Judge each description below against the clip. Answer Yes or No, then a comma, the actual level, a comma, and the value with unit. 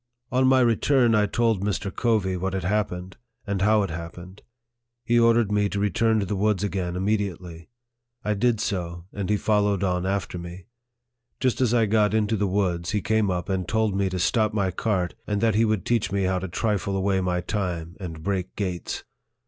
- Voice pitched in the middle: No, low, 100 Hz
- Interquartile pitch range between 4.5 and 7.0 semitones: No, average, 2.8 semitones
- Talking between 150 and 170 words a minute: No, fast, 205 wpm